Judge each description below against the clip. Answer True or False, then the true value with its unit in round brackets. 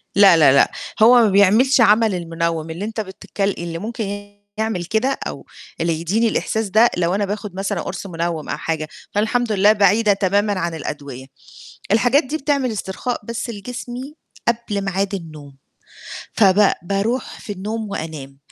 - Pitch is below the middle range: False (200 Hz)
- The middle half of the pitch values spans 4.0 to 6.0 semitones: True (4.5 semitones)